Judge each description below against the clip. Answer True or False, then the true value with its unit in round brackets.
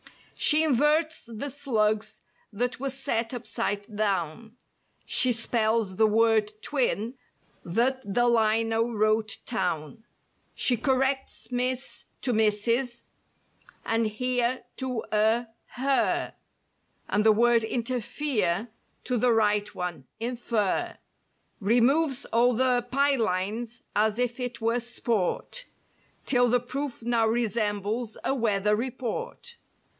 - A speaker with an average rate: False (110 wpm)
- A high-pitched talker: True (235 Hz)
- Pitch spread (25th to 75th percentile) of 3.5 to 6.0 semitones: False (2.7 semitones)